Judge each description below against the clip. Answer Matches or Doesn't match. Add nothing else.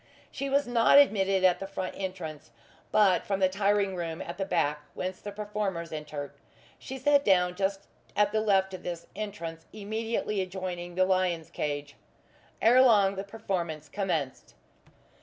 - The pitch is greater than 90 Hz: Matches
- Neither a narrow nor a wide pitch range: Matches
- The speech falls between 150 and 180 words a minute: Matches